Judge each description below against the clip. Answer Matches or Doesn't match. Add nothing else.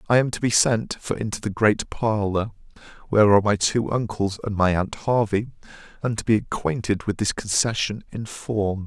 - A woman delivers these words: Doesn't match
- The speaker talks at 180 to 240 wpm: Matches